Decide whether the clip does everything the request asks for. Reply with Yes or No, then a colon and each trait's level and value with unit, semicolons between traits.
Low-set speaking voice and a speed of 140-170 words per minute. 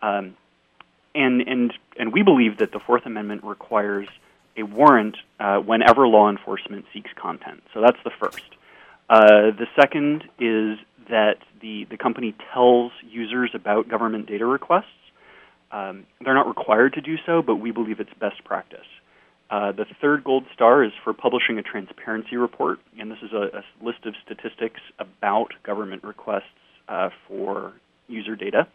Yes: low, 110 Hz; average, 160 wpm